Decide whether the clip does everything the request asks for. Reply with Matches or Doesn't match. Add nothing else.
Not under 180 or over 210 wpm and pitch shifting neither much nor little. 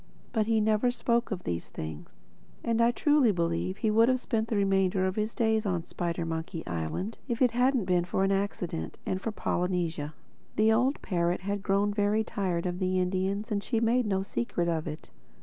Matches